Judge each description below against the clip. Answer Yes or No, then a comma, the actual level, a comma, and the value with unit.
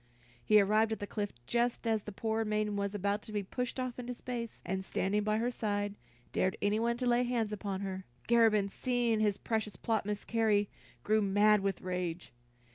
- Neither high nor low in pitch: No, high, 215 Hz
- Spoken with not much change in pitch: Yes, narrow, 2.3 semitones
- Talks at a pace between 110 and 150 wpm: No, average, 190 wpm